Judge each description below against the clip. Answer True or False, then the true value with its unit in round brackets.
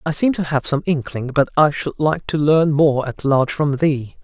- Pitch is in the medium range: True (145 Hz)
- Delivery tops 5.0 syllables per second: False (4.8 syllables/s)